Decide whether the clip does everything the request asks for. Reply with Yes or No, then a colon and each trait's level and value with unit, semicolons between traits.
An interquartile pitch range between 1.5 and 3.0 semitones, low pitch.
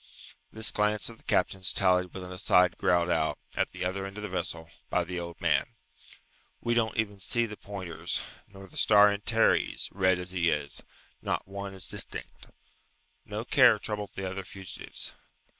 Yes: narrow, 2.6 semitones; very low, 95 Hz